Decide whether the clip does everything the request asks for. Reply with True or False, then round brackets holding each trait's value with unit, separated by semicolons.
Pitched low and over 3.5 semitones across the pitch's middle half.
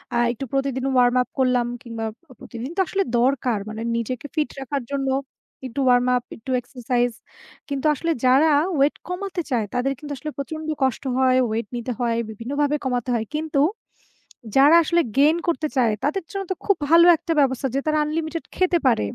False (270 Hz; 3.9 semitones)